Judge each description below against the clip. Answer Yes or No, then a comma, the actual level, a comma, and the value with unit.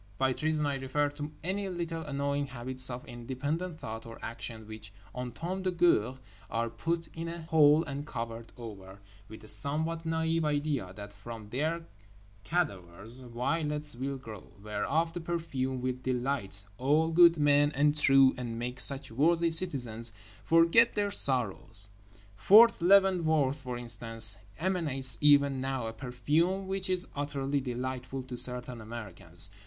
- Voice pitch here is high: No, low, 135 Hz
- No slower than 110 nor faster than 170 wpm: Yes, average, 150 wpm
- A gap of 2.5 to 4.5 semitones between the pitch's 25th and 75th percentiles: No, wide, 5.4 semitones